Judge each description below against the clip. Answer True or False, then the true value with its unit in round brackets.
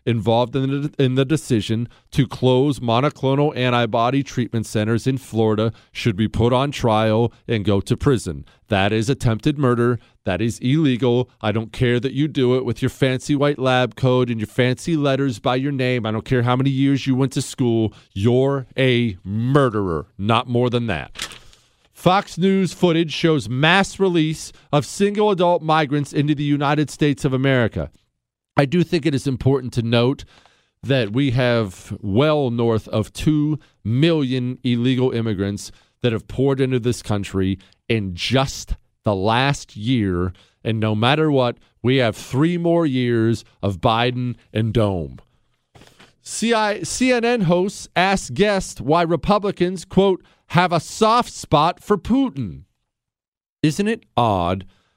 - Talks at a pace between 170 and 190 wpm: False (155 wpm)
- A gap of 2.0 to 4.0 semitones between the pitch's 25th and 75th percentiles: False (4.5 semitones)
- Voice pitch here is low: True (125 Hz)